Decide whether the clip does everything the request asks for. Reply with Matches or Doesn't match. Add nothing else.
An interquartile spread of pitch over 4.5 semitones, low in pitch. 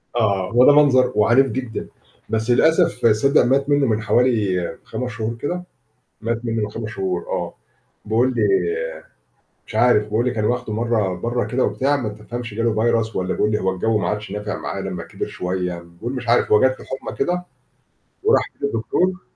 Doesn't match